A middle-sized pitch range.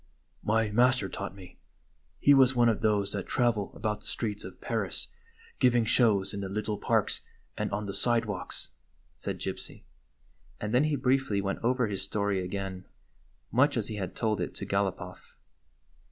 Yes: average, 3.4 semitones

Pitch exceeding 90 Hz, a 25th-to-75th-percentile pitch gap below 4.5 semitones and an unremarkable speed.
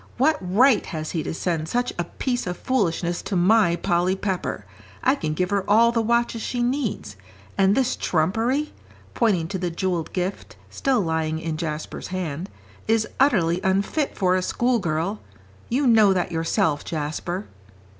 No: high, 190 Hz; wide, 5.6 semitones; average, 160 wpm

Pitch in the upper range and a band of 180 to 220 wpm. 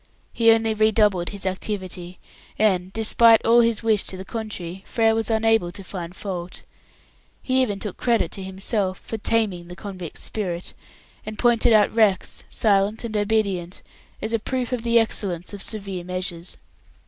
No: high, 205 Hz; average, 160 wpm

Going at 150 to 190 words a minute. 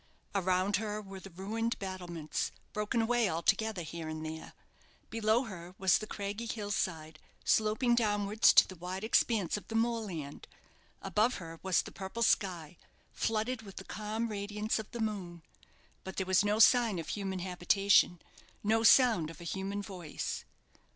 Yes: average, 160 wpm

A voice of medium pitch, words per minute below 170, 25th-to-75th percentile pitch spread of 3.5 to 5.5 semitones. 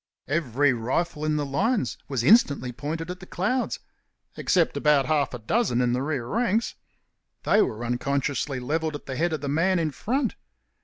No: medium, 150 Hz; average, 175 wpm; average, 5.0 semitones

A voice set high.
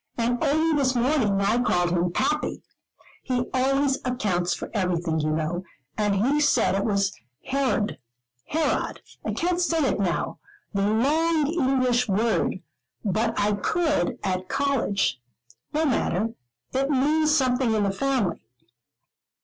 Yes: high, 245 Hz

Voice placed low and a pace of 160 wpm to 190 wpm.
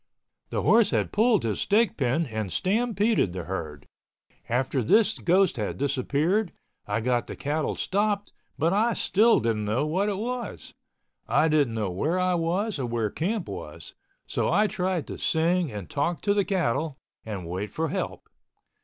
No: medium, 160 Hz; average, 170 wpm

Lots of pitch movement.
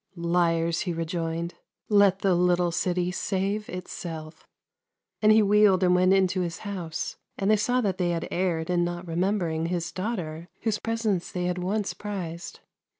No: average, 2.7 semitones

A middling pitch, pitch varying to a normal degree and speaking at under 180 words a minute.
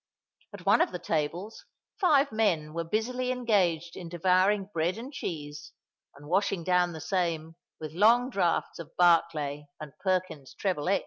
Yes: medium, 180 Hz; average, 4.2 semitones; average, 155 wpm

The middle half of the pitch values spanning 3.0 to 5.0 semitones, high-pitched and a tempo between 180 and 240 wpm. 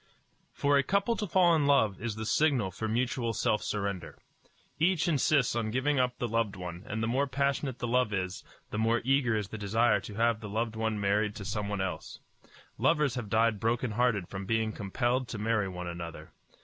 No: average, 3.7 semitones; low, 115 Hz; average, 200 wpm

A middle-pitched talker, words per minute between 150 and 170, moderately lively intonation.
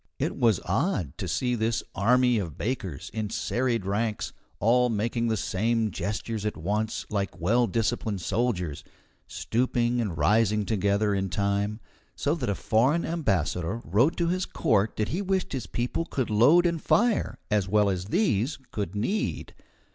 No: low, 110 Hz; average, 160 wpm; average, 3.7 semitones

